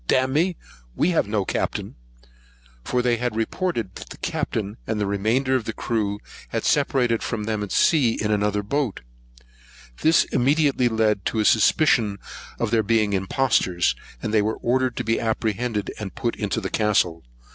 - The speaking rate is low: No, average, 165 wpm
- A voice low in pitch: Yes, low, 110 Hz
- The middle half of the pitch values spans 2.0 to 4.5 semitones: Yes, average, 3.5 semitones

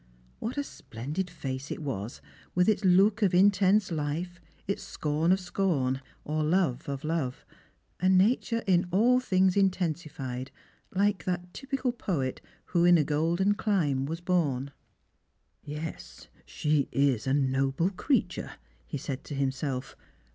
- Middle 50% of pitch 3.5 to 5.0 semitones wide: No, wide, 5.4 semitones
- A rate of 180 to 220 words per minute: No, average, 145 wpm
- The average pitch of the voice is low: No, medium, 170 Hz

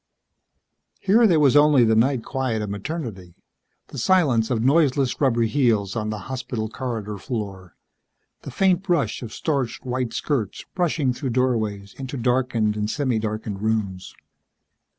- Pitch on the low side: Yes, low, 120 Hz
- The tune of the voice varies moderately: Yes, average, 4.3 semitones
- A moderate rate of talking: Yes, average, 145 wpm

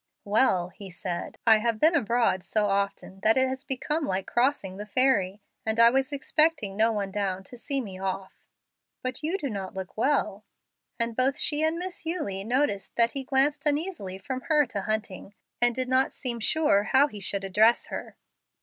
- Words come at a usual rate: Yes, average, 190 wpm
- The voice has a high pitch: Yes, high, 230 Hz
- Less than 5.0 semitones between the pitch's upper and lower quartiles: No, wide, 5.6 semitones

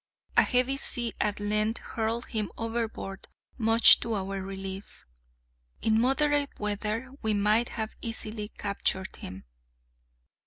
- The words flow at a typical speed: No, slow, 120 wpm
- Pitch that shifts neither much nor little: No, narrow, 2.3 semitones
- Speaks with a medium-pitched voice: No, high, 220 Hz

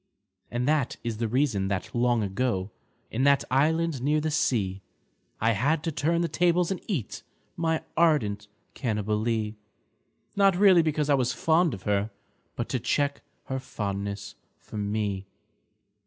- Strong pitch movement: Yes, wide, 7.0 semitones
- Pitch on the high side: No, low, 125 Hz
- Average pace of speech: Yes, average, 155 wpm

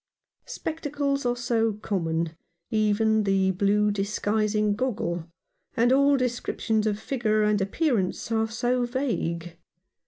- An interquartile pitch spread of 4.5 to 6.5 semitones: No, average, 3.4 semitones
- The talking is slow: Yes, slow, 125 wpm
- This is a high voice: Yes, high, 215 Hz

